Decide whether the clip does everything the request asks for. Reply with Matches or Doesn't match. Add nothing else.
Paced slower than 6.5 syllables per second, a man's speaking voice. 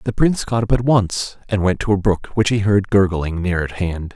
Matches